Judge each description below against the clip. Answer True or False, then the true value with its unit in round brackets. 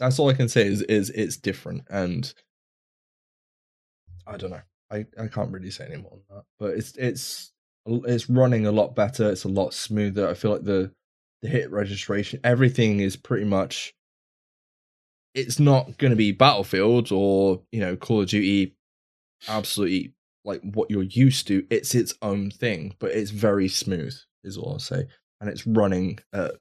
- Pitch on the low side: True (105 Hz)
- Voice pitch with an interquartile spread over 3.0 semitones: True (3.9 semitones)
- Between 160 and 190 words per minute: True (180 wpm)